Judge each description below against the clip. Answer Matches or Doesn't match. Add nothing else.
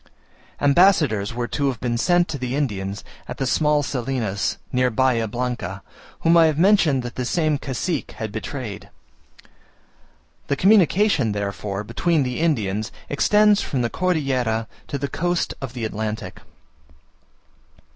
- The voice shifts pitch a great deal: Matches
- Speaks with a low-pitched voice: Matches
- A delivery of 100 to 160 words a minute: Matches